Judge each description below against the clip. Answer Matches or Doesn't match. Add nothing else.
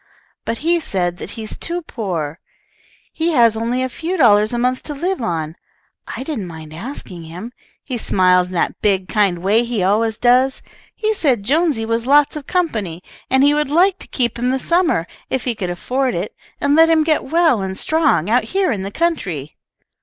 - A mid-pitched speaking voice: Doesn't match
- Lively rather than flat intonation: Matches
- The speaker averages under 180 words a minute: Doesn't match